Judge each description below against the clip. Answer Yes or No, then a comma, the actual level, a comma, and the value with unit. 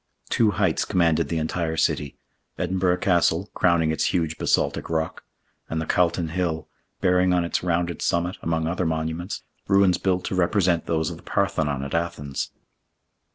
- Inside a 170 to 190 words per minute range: No, average, 155 wpm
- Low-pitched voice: Yes, very low, 85 Hz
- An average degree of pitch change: No, narrow, 2.1 semitones